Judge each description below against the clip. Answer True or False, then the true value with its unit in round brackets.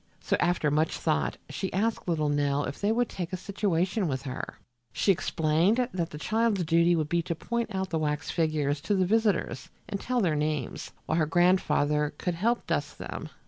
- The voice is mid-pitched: True (170 Hz)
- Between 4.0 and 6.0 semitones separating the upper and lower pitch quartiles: True (4.5 semitones)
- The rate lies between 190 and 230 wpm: True (195 wpm)